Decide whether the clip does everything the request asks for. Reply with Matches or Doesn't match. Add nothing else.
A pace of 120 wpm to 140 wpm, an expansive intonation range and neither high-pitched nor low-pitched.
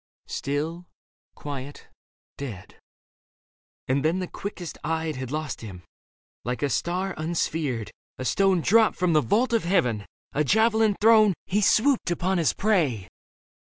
Matches